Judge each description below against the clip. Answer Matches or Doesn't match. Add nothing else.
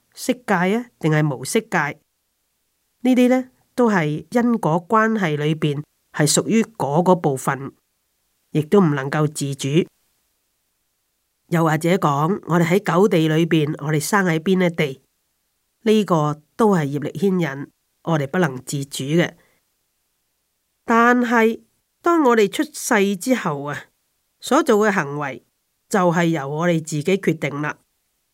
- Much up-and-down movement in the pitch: Matches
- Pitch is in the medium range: Matches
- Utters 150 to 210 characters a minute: Matches